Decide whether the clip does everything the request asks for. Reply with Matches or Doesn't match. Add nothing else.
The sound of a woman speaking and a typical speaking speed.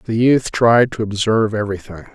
Doesn't match